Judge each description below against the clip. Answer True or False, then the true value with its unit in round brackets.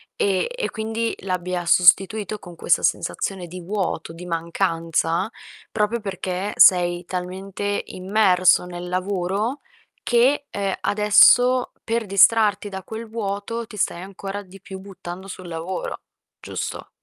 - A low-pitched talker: False (195 Hz)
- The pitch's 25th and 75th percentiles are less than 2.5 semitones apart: False (2.8 semitones)